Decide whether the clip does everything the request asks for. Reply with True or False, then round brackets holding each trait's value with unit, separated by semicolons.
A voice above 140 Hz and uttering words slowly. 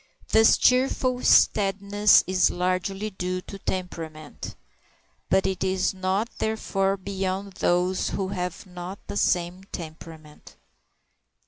True (190 Hz; 110 wpm)